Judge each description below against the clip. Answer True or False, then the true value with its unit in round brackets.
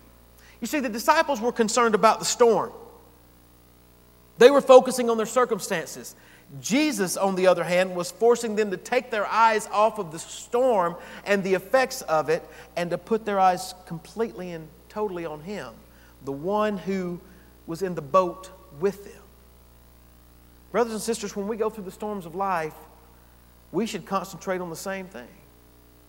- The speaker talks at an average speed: True (170 wpm)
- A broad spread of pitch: True (8.6 semitones)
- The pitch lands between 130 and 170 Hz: False (185 Hz)